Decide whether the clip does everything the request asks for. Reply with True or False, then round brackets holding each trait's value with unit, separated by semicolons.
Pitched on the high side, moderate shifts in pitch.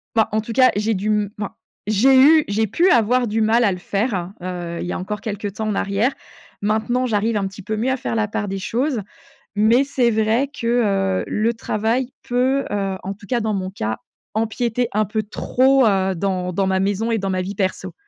True (215 Hz; 3.2 semitones)